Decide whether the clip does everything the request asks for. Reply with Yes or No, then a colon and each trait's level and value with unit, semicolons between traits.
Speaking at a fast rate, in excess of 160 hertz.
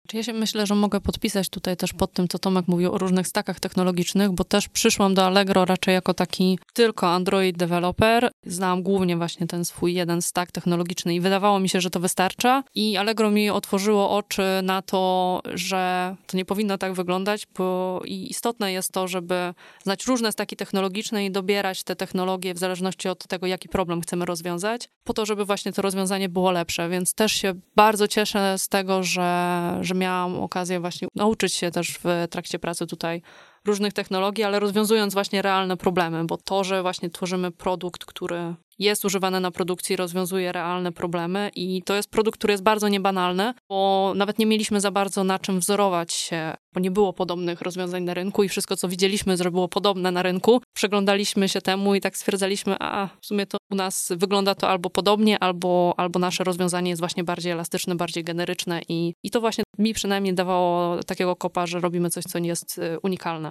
Yes: fast, 190 wpm; high, 190 Hz